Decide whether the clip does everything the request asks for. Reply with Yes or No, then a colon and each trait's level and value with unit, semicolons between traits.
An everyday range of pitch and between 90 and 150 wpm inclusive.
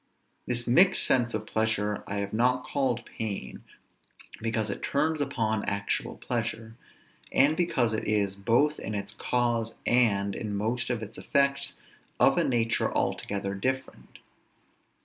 Yes: average, 3.2 semitones; average, 140 wpm